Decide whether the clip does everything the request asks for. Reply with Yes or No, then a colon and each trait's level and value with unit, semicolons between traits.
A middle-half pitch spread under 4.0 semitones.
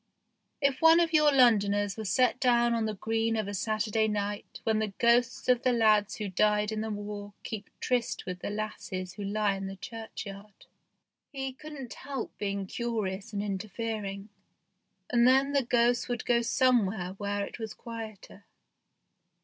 Yes: average, 2.9 semitones